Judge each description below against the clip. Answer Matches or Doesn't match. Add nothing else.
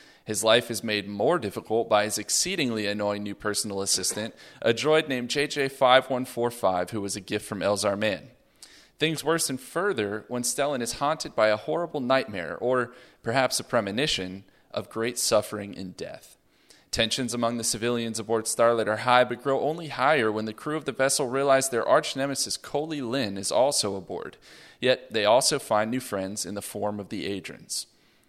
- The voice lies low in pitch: Matches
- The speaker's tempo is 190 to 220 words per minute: Doesn't match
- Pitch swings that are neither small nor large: Matches